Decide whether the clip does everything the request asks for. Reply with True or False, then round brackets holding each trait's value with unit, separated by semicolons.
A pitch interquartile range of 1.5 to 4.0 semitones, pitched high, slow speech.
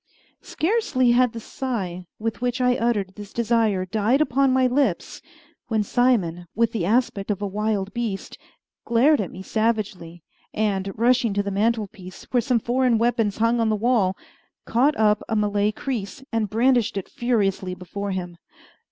False (3.5 semitones; 220 Hz; 160 wpm)